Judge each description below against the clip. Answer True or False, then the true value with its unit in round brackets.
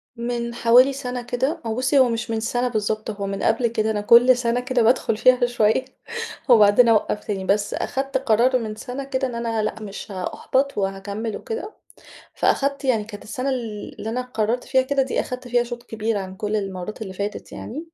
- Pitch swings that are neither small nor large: True (3.0 semitones)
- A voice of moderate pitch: False (235 Hz)